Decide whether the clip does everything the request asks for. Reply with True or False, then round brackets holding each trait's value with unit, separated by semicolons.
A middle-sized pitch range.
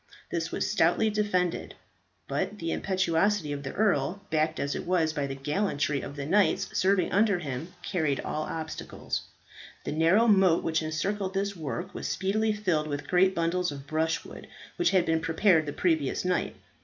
True (4.1 semitones)